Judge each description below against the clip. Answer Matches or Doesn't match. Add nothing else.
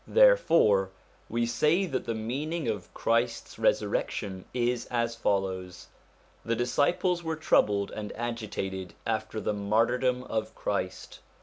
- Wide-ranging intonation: Doesn't match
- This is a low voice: Matches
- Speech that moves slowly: Matches